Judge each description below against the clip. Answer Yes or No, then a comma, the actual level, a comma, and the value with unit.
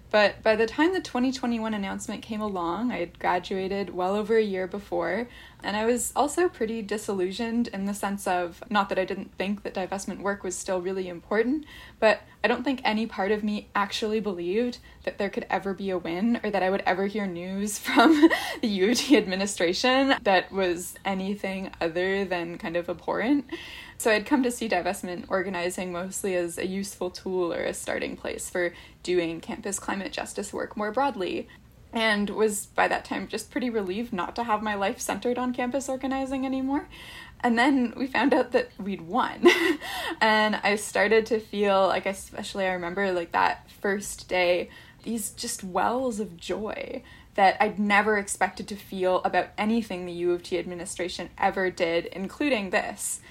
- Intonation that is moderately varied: Yes, average, 4.0 semitones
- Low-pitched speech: No, high, 205 Hz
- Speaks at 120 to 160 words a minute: No, average, 180 wpm